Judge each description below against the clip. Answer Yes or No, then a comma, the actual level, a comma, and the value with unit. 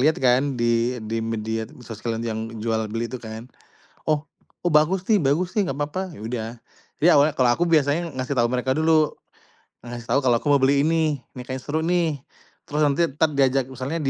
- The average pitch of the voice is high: No, low, 135 Hz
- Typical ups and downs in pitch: Yes, average, 4.7 semitones